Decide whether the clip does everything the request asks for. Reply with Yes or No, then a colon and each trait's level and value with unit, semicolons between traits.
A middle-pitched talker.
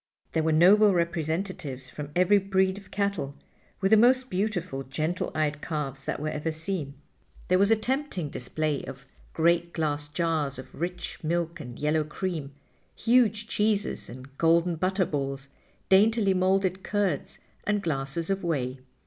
Yes: medium, 170 Hz